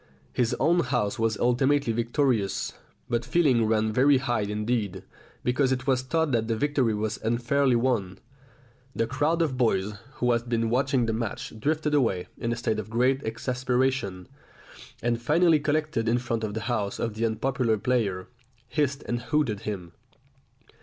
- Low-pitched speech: Yes, low, 120 Hz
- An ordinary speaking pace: Yes, average, 160 wpm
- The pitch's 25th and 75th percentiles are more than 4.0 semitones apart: No, average, 3.2 semitones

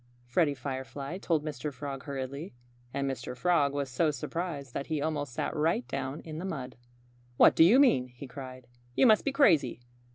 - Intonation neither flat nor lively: Yes, average, 3.8 semitones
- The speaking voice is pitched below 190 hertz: Yes, medium, 140 Hz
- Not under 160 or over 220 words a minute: Yes, average, 185 wpm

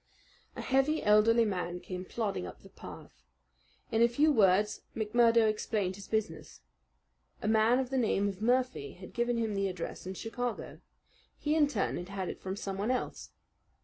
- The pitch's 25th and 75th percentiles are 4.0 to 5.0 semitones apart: No, average, 3.6 semitones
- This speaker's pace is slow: No, average, 175 wpm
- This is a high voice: Yes, high, 215 Hz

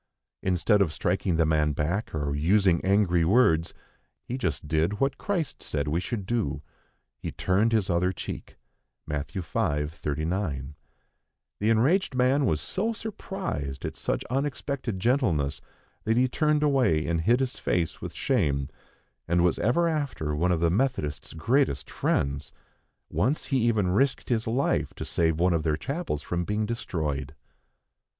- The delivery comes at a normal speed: Yes, average, 155 wpm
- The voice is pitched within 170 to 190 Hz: No, very low, 95 Hz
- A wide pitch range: Yes, wide, 8.2 semitones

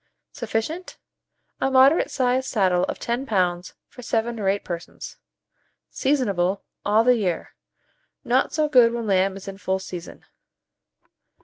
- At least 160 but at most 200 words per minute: No, slow, 135 wpm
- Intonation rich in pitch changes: No, average, 5.0 semitones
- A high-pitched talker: Yes, high, 220 Hz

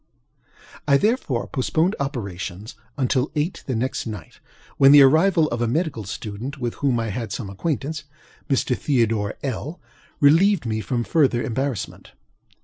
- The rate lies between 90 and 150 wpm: Yes, average, 145 wpm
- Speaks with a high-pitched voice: No, low, 130 Hz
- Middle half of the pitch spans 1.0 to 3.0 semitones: No, average, 4.6 semitones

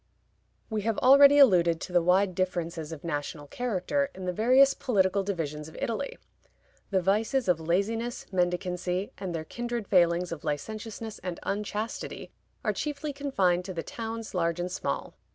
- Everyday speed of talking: Yes, average, 155 wpm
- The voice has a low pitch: No, high, 190 Hz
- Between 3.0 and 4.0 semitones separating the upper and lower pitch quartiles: No, average, 4.6 semitones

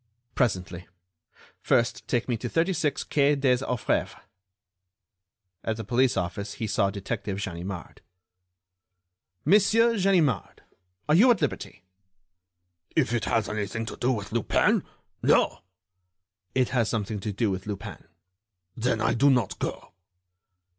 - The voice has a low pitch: Yes, low, 115 Hz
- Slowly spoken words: Yes, slow, 125 wpm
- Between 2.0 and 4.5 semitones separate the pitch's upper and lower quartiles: No, average, 5.2 semitones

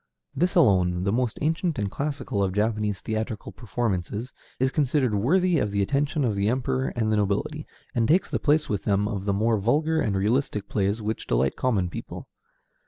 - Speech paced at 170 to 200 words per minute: Yes, average, 185 wpm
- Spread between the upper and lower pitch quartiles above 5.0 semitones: Yes, wide, 5.6 semitones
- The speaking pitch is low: Yes, low, 110 Hz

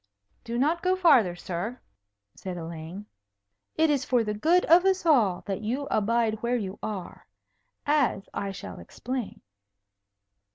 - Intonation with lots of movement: Yes, wide, 6.9 semitones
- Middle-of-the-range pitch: No, high, 230 Hz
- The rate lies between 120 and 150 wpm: Yes, average, 140 wpm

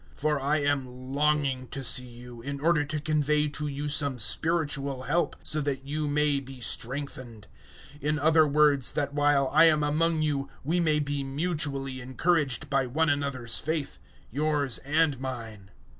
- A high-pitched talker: No, medium, 145 Hz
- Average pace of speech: Yes, average, 170 wpm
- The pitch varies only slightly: Yes, narrow, 2.3 semitones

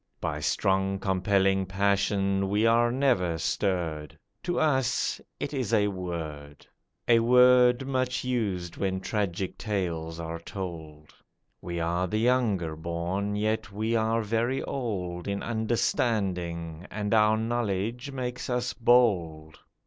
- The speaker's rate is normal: No, slow, 125 wpm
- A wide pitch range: No, average, 5.0 semitones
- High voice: No, low, 100 Hz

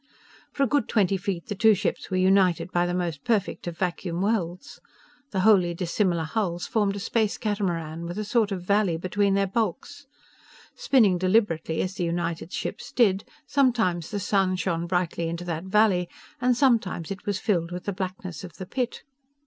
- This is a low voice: No, medium, 185 Hz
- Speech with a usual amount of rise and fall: Yes, average, 3.2 semitones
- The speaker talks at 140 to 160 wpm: No, average, 180 wpm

